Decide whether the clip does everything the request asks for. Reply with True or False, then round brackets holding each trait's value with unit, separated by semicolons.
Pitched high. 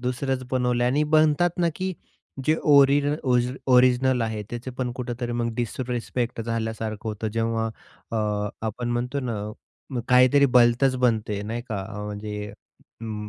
False (120 Hz)